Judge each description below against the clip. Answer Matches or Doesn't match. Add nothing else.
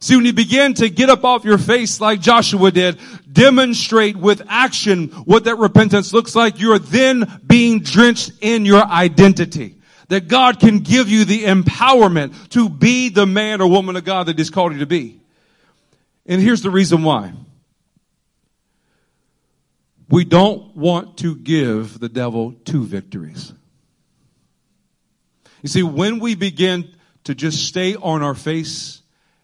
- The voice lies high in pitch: Matches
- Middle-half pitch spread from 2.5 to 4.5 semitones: Doesn't match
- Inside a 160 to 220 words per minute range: Doesn't match